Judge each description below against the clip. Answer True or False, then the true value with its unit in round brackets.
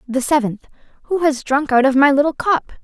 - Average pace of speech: False (210 wpm)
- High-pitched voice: True (280 Hz)